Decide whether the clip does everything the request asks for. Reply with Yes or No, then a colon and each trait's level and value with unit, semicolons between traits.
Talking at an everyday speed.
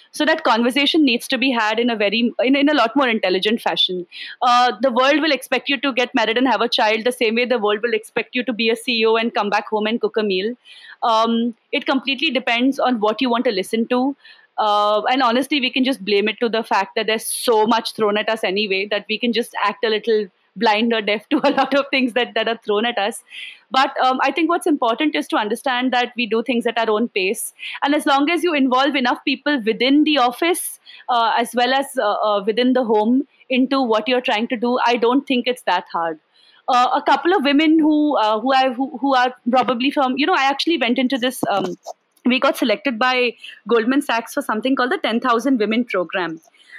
No: fast, 235 wpm